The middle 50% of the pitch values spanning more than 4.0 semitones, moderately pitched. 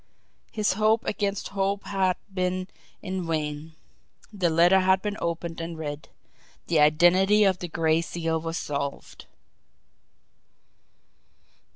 No: average, 3.0 semitones; medium, 175 Hz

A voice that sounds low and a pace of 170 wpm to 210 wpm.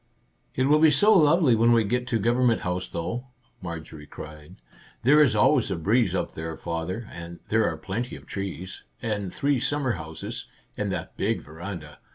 Yes: low, 105 Hz; average, 190 wpm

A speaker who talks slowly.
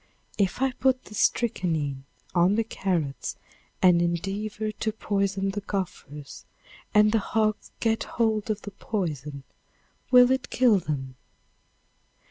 Yes: slow, 125 wpm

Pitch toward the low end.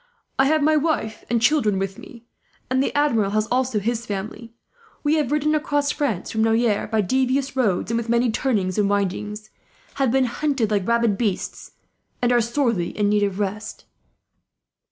No: high, 235 Hz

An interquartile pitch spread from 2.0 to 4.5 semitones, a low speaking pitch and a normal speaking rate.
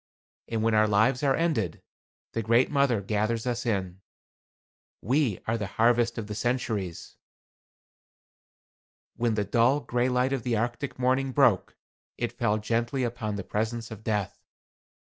Yes: narrow, 2.6 semitones; low, 115 Hz; average, 150 wpm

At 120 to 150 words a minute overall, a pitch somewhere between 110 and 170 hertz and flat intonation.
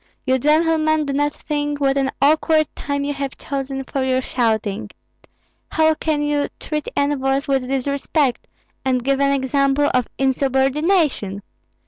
No: average, 140 wpm; very high, 275 Hz; narrow, 1.8 semitones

